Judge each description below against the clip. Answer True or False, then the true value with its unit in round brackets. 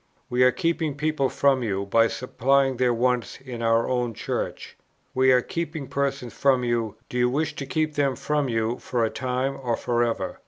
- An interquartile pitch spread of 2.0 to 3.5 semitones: True (2.7 semitones)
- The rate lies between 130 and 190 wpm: False (200 wpm)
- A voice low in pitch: True (125 Hz)